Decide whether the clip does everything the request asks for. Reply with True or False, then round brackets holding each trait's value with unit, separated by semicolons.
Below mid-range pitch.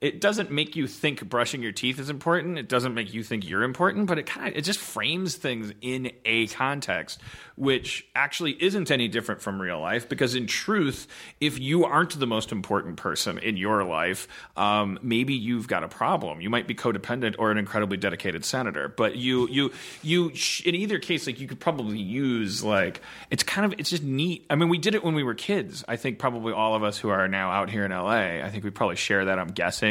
True (125 Hz)